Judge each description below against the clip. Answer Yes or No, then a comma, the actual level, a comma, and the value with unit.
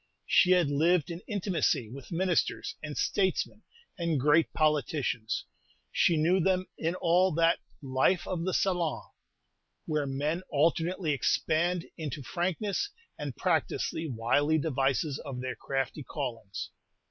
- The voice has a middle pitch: Yes, medium, 160 Hz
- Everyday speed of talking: No, slow, 130 wpm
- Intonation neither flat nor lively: Yes, average, 4.0 semitones